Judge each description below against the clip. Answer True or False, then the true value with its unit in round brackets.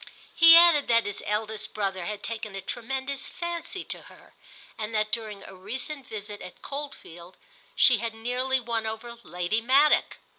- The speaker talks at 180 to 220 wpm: False (160 wpm)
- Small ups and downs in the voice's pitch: False (4.1 semitones)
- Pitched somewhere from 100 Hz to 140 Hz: False (225 Hz)